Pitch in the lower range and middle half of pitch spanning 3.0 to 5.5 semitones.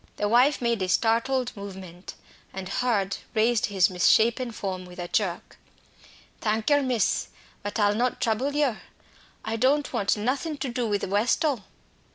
No: high, 225 Hz; average, 4.1 semitones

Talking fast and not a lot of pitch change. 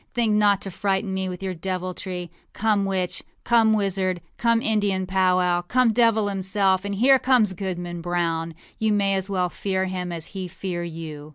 No: average, 175 wpm; narrow, 2.3 semitones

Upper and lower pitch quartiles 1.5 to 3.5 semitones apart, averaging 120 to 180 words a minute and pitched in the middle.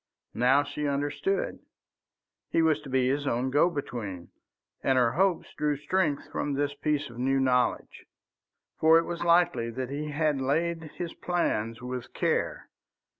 No: average, 4.2 semitones; average, 155 wpm; medium, 145 Hz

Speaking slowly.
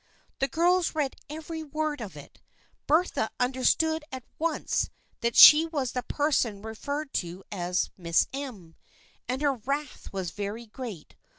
No: average, 155 wpm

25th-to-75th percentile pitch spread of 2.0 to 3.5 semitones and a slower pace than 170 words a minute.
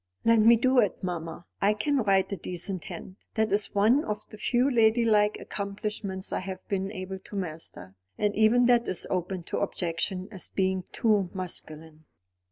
No: average, 2.9 semitones; average, 175 wpm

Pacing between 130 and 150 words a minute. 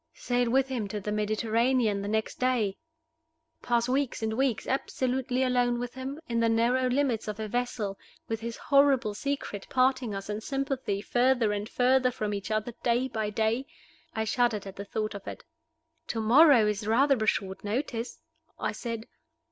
No: average, 175 wpm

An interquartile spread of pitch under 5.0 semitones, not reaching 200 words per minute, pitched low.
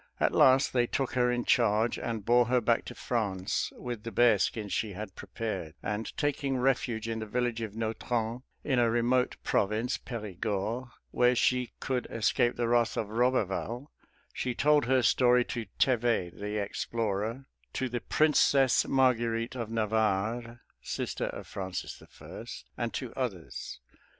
Yes: narrow, 2.4 semitones; average, 150 wpm; low, 115 Hz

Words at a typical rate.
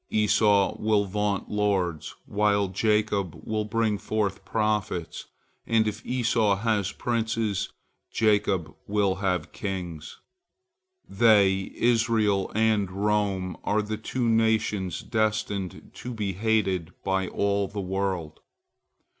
No: slow, 110 wpm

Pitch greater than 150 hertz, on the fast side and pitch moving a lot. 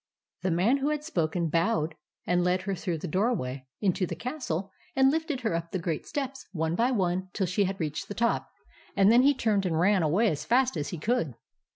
Yes: high, 190 Hz; fast, 220 wpm; wide, 6.2 semitones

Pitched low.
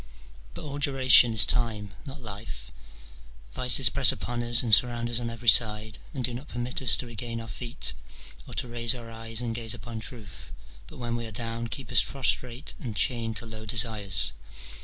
Yes: low, 115 Hz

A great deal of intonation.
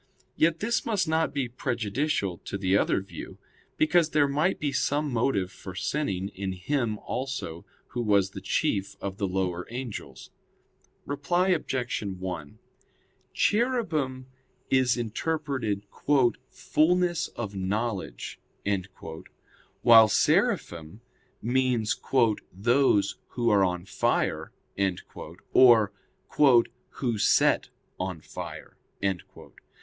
Yes: wide, 6.8 semitones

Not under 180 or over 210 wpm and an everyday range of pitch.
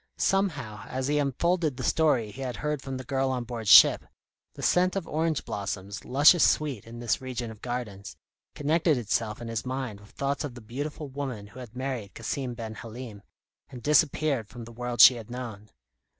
Yes: average, 195 wpm; average, 4.0 semitones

